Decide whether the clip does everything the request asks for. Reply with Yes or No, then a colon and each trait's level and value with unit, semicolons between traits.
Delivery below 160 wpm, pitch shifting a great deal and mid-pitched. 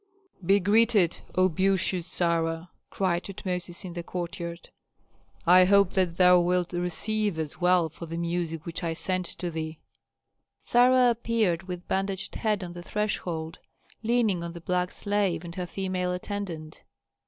No: average, 150 wpm; narrow, 2.5 semitones; medium, 180 Hz